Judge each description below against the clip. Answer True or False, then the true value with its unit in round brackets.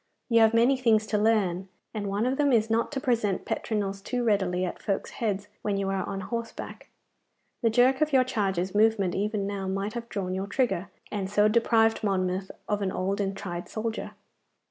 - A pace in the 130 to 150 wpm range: False (195 wpm)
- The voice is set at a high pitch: True (210 Hz)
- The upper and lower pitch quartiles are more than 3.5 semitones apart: False (2.9 semitones)